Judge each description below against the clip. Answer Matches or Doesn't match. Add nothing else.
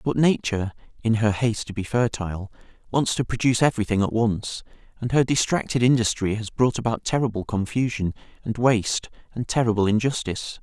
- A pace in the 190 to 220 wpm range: Doesn't match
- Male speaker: Matches